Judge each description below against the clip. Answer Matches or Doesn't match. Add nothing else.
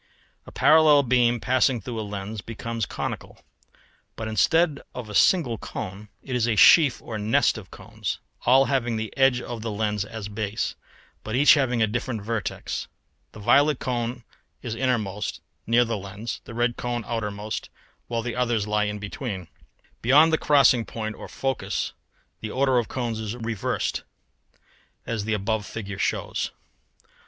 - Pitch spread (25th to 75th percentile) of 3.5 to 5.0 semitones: Doesn't match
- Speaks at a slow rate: Doesn't match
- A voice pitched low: Matches